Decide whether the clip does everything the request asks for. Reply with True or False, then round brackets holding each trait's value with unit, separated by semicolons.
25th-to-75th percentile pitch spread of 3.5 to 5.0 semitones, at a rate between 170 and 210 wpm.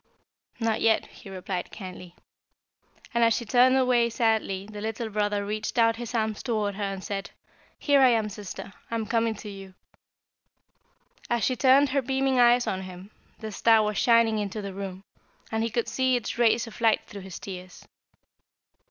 False (3.0 semitones; 180 wpm)